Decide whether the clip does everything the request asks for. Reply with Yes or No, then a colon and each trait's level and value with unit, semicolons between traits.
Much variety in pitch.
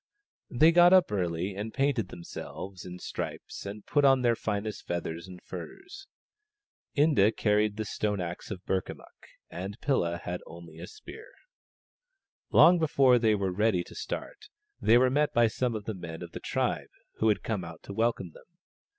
Yes: wide, 6.0 semitones